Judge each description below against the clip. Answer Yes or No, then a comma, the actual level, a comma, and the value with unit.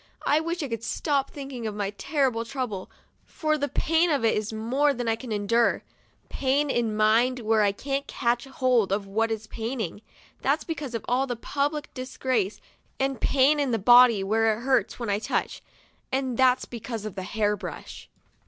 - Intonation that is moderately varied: Yes, average, 3.9 semitones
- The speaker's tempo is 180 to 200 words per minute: Yes, average, 185 wpm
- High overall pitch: Yes, high, 240 Hz